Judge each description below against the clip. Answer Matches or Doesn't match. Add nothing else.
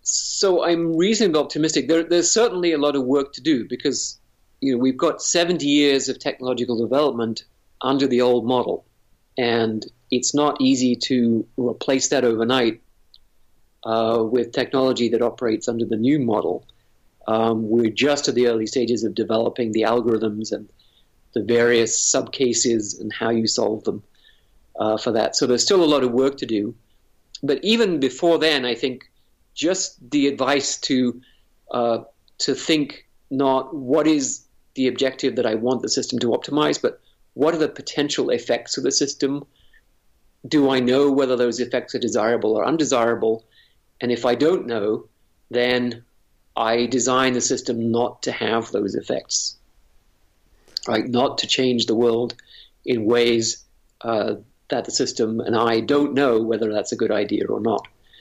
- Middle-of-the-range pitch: Doesn't match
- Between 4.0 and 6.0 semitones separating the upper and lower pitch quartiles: Doesn't match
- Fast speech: Doesn't match